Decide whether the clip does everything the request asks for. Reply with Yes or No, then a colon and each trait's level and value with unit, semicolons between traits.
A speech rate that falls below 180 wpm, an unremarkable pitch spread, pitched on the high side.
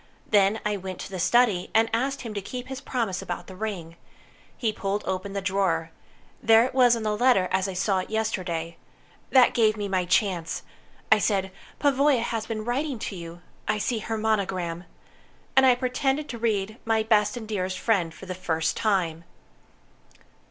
No: average, 185 wpm; average, 3.8 semitones; high, 210 Hz